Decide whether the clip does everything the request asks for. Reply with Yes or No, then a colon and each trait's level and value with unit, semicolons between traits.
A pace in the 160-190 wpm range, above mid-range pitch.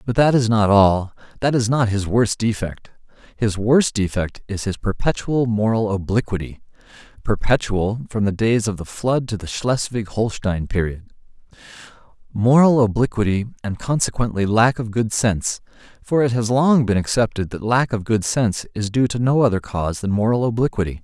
No: average, 165 wpm; low, 110 Hz